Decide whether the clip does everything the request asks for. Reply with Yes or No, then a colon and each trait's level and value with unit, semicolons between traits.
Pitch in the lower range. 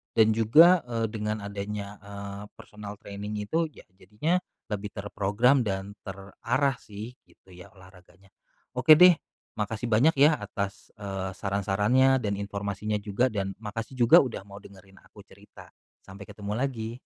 Yes: low, 105 Hz